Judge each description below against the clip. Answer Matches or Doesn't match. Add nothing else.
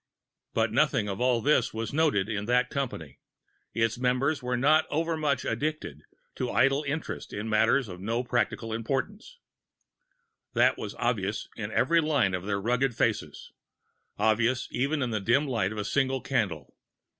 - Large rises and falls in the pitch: Doesn't match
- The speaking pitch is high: Doesn't match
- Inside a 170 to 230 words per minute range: Doesn't match